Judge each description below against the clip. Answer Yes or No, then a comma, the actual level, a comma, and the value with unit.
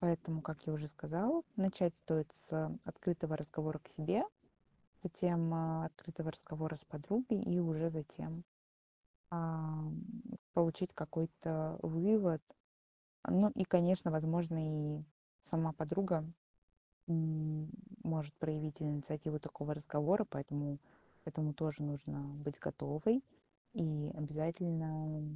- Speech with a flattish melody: Yes, narrow, 1.8 semitones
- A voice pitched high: No, medium, 160 Hz